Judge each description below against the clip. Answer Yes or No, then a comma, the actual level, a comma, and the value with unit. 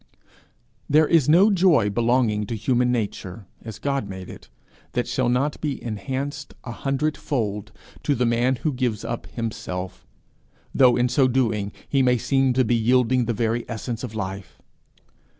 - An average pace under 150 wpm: No, average, 160 wpm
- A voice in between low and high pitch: No, low, 120 Hz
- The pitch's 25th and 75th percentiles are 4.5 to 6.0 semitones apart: No, average, 3.4 semitones